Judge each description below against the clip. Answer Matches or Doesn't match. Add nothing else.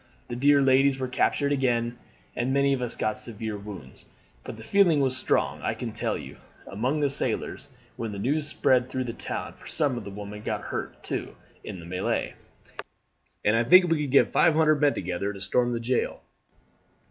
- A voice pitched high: Doesn't match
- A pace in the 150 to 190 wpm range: Doesn't match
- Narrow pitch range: Doesn't match